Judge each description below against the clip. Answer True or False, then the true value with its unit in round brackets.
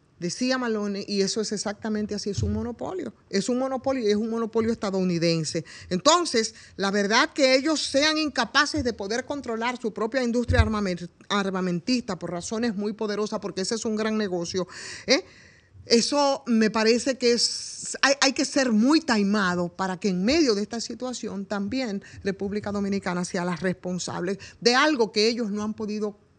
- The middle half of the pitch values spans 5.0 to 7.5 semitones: False (3.8 semitones)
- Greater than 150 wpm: True (165 wpm)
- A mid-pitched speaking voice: False (215 Hz)